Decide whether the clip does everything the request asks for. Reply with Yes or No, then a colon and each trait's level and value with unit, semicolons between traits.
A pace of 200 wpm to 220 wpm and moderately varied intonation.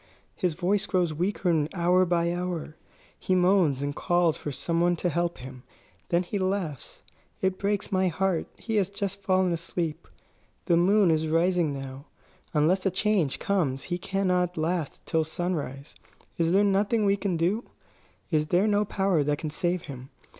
No: average, 170 wpm; average, 3.1 semitones